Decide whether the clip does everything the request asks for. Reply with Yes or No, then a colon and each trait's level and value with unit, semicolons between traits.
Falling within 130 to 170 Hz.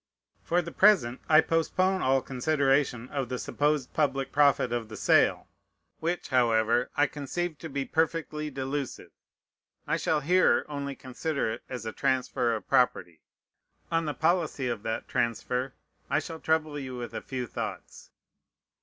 Yes: medium, 140 Hz